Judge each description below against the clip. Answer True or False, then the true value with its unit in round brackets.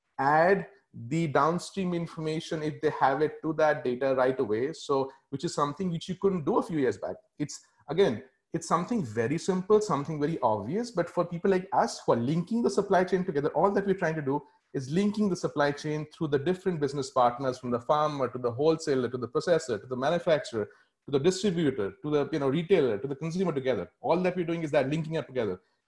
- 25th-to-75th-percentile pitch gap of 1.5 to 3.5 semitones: False (3.9 semitones)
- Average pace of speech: False (220 wpm)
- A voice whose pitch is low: False (160 Hz)